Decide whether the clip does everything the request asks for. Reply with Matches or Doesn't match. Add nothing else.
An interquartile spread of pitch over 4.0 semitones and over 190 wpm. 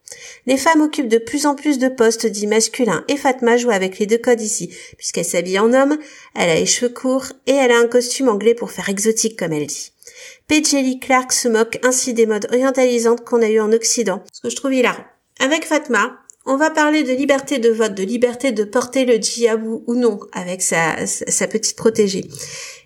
Doesn't match